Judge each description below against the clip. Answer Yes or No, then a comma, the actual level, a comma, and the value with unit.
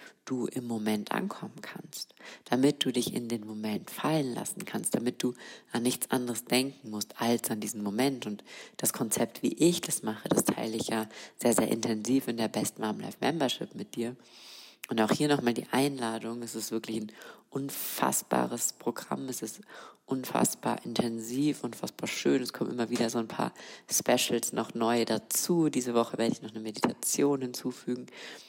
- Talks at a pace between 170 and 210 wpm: Yes, average, 175 wpm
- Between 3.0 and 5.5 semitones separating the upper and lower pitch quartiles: No, narrow, 2.4 semitones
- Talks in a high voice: No, low, 120 Hz